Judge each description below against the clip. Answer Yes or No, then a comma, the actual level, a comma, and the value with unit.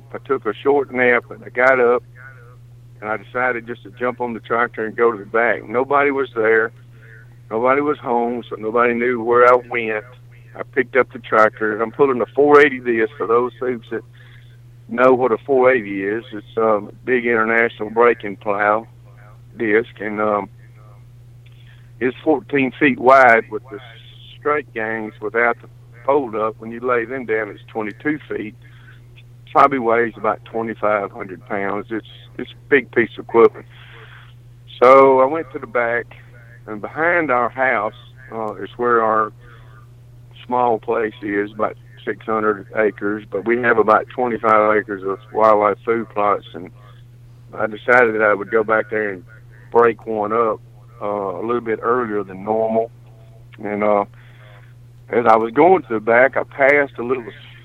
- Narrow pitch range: Yes, narrow, 1.9 semitones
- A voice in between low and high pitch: No, low, 120 Hz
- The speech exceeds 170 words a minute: No, average, 165 wpm